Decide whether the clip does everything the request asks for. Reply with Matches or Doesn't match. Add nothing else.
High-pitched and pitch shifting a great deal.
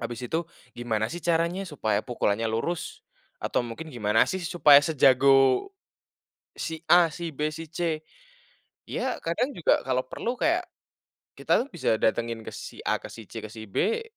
Doesn't match